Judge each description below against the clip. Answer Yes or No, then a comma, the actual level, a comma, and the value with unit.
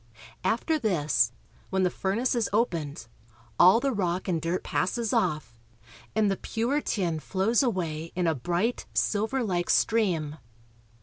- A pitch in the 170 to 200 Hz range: Yes, medium, 185 Hz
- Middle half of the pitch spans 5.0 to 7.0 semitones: Yes, average, 5.3 semitones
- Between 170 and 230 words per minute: No, slow, 135 wpm